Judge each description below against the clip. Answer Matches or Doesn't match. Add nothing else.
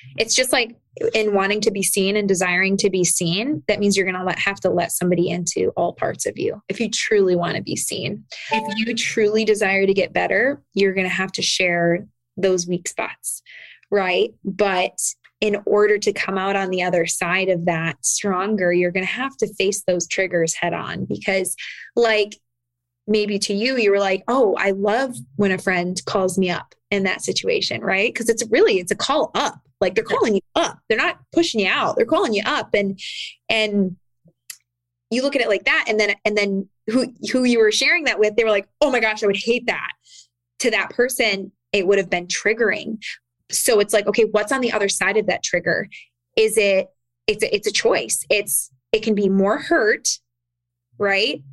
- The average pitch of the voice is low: Doesn't match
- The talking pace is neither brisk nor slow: Doesn't match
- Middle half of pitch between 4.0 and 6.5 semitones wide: Doesn't match